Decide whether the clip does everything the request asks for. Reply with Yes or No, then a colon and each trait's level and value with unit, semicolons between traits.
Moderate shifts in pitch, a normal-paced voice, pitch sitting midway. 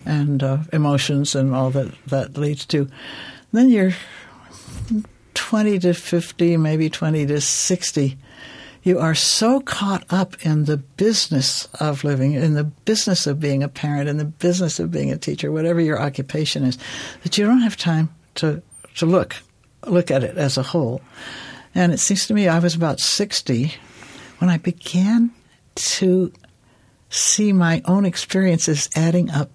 Yes: average, 4.3 semitones; average, 160 wpm; medium, 160 Hz